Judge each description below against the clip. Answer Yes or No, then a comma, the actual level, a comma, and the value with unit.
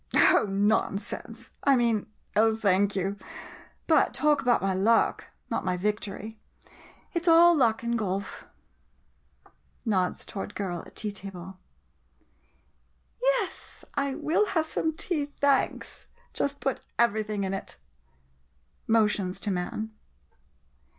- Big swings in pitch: Yes, wide, 6.0 semitones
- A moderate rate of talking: No, slow, 130 wpm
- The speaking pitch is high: Yes, high, 220 Hz